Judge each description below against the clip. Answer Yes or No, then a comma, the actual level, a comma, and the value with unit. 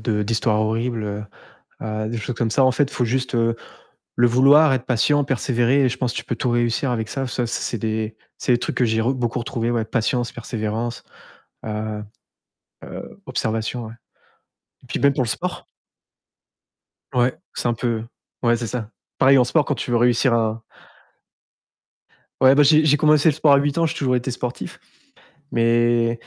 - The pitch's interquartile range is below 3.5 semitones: Yes, average, 2.7 semitones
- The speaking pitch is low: Yes, low, 120 Hz